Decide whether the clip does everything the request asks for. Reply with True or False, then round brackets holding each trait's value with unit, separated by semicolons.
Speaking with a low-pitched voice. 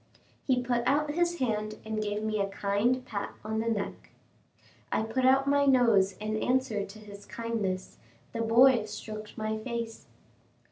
False (220 Hz)